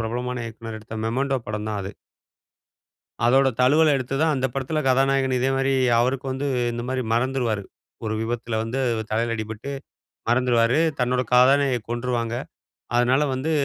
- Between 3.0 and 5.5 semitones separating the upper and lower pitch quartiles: No, narrow, 2.6 semitones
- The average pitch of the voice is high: No, low, 125 Hz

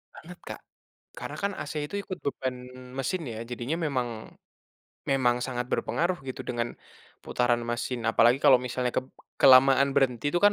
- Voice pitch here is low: Yes, low, 130 Hz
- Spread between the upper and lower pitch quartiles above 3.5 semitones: No, average, 2.9 semitones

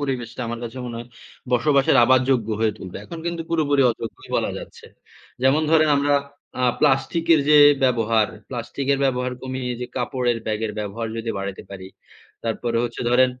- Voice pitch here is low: Yes, low, 125 Hz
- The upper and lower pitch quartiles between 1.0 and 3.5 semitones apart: Yes, average, 3.1 semitones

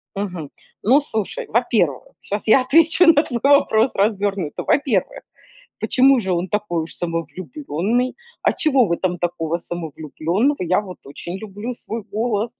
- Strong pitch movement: Yes, wide, 5.9 semitones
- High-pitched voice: Yes, high, 205 Hz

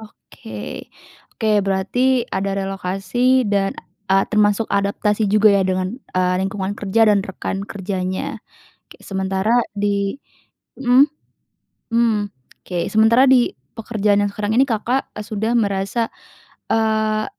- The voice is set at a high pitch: Yes, high, 205 Hz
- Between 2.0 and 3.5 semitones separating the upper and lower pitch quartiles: Yes, narrow, 2.5 semitones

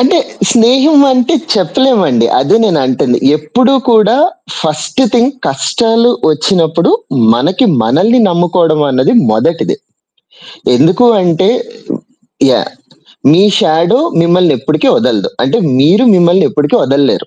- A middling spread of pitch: No, wide, 7.3 semitones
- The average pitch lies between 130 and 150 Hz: No, medium, 175 Hz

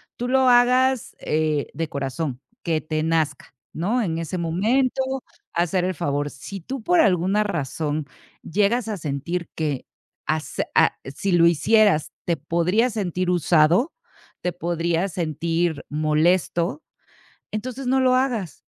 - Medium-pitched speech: Yes, medium, 175 Hz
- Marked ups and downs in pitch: Yes, wide, 5.8 semitones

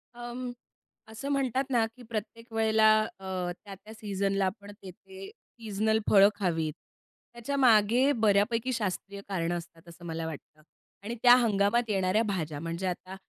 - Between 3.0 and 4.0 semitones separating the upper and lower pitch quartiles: Yes, average, 3.7 semitones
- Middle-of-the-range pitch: No, high, 205 Hz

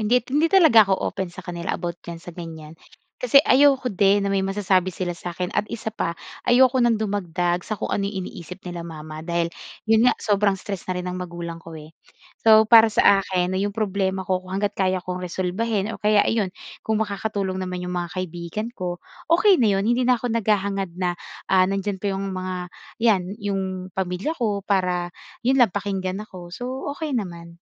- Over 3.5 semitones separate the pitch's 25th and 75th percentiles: No, average, 3.2 semitones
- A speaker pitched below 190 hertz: No, high, 195 Hz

